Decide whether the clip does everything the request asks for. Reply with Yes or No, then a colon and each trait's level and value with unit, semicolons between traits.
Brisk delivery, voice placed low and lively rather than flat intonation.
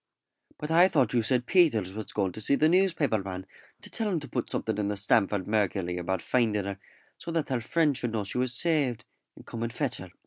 Yes: fast, 235 wpm; low, 115 Hz; wide, 6.7 semitones